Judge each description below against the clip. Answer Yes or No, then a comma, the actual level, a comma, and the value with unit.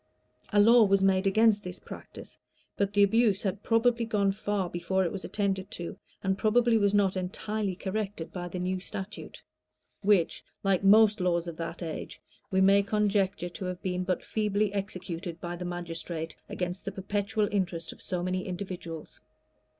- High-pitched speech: Yes, high, 195 Hz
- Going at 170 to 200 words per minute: Yes, average, 175 wpm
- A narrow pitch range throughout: Yes, narrow, 2.3 semitones